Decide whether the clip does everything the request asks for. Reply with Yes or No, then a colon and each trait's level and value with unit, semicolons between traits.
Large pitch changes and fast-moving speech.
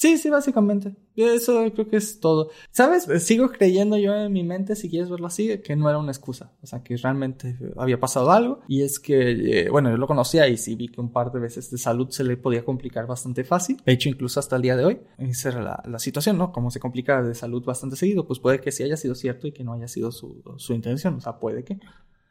Yes: wide, 7.7 semitones; fast, 255 wpm